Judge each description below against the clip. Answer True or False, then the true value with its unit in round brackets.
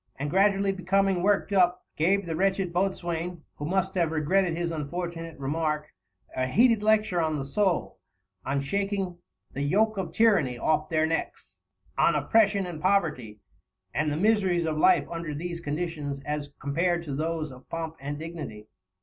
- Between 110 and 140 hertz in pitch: False (170 Hz)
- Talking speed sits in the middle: True (160 wpm)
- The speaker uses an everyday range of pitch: True (4.1 semitones)